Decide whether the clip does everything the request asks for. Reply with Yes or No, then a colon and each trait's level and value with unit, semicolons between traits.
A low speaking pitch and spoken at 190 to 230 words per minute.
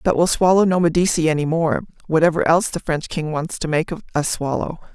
No: medium, 165 Hz; fast, 205 wpm